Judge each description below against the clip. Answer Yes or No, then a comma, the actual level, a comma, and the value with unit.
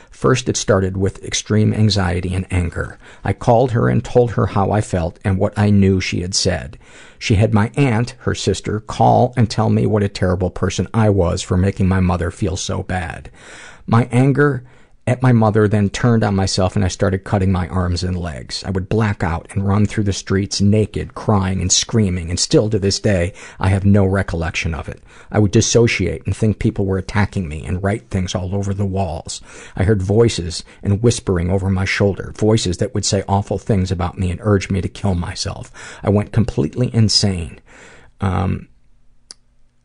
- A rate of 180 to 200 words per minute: Yes, average, 195 wpm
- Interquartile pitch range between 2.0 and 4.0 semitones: Yes, narrow, 2.5 semitones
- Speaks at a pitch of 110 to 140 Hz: No, low, 100 Hz